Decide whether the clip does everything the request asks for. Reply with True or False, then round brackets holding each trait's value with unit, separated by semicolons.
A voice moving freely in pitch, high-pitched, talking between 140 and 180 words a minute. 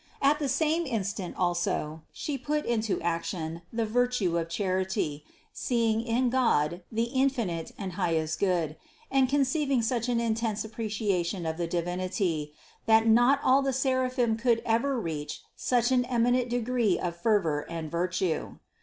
True (6.1 semitones; 220 Hz; 150 wpm)